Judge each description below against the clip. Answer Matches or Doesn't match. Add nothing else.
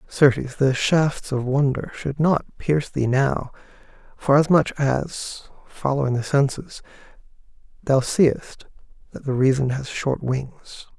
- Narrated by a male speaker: Matches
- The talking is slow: Matches